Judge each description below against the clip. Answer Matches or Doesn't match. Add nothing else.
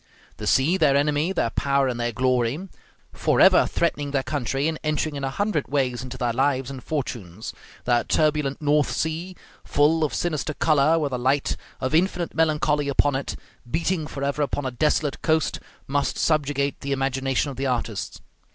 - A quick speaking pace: Doesn't match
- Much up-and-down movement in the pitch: Doesn't match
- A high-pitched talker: Doesn't match